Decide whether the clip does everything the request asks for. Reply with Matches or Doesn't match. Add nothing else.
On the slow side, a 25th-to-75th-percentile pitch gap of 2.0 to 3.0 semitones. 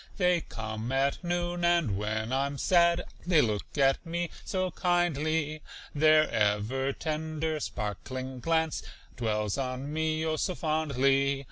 Doesn't match